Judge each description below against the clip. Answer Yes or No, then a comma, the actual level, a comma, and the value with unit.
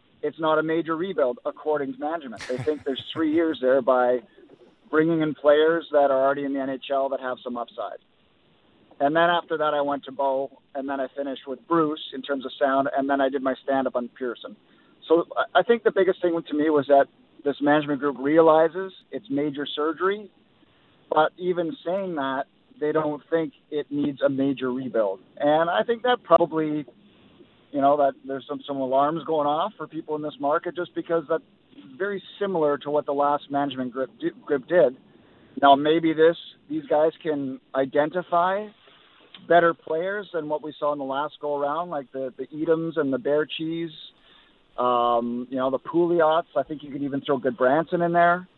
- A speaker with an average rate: Yes, average, 195 wpm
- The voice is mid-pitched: Yes, medium, 150 Hz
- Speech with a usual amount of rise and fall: Yes, average, 3.3 semitones